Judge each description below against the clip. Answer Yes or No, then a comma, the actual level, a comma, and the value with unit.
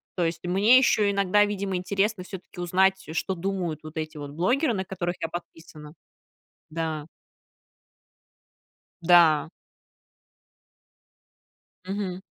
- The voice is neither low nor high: Yes, medium, 180 Hz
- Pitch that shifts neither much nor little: Yes, average, 3.1 semitones